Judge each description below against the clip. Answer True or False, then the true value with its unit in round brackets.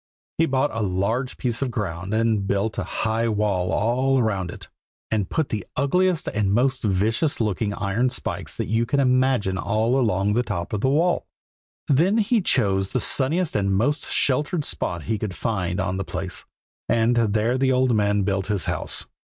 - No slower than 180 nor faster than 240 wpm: True (185 wpm)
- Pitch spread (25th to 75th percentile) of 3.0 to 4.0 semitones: False (4.7 semitones)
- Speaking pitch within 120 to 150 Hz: False (110 Hz)